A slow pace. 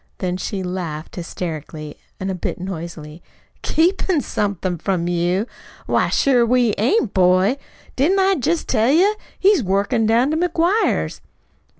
Yes: slow, 130 wpm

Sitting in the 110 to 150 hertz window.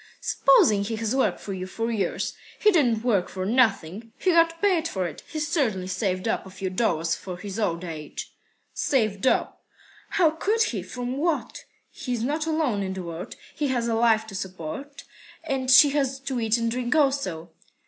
No: high, 230 Hz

